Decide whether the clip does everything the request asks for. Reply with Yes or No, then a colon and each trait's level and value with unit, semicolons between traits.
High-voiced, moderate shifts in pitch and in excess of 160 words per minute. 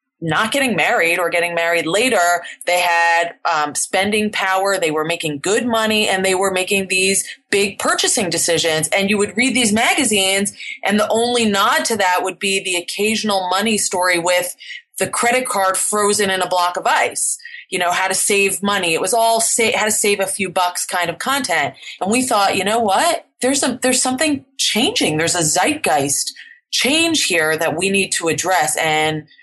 Yes: high, 195 Hz; average, 4.5 semitones; average, 190 wpm